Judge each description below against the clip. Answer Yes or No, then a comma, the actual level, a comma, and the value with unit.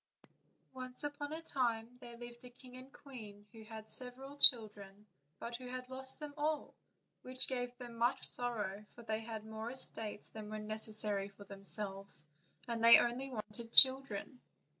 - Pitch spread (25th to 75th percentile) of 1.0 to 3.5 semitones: Yes, average, 3.0 semitones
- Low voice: No, high, 235 Hz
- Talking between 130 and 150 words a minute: No, average, 160 wpm